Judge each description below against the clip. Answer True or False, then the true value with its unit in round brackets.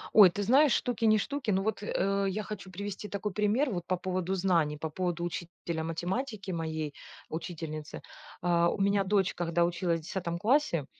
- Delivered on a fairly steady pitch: False (3.3 semitones)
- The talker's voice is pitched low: False (185 Hz)